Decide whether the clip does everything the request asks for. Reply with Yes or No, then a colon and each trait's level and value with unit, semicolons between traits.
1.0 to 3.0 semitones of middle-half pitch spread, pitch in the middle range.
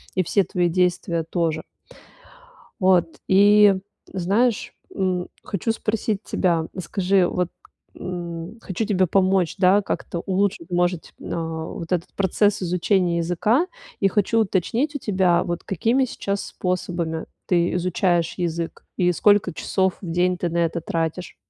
Yes: narrow, 2.5 semitones; medium, 180 Hz